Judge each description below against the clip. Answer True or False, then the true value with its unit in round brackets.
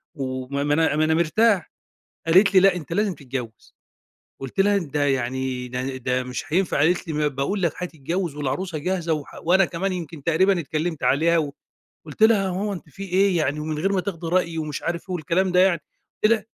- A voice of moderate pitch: True (165 Hz)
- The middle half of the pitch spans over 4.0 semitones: True (4.5 semitones)